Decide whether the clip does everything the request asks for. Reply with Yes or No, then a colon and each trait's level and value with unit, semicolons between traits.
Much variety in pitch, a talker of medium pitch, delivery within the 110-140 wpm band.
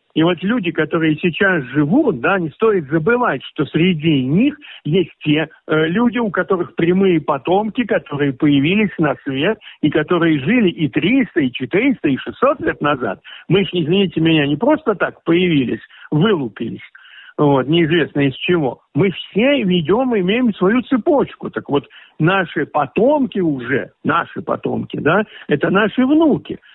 No: wide, 5.8 semitones; medium, 175 Hz; average, 150 wpm